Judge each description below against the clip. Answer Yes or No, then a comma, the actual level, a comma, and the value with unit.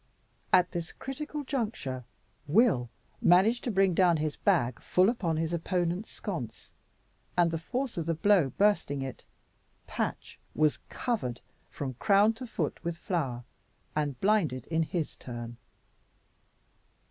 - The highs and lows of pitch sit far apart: Yes, wide, 6.2 semitones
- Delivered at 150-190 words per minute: No, slow, 135 wpm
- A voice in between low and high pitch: Yes, medium, 170 Hz